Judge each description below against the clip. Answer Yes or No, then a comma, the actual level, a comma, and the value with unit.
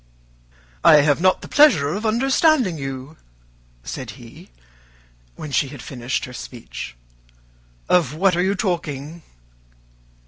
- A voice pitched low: No, medium, 155 Hz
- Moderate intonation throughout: No, wide, 6.0 semitones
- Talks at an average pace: No, slow, 125 wpm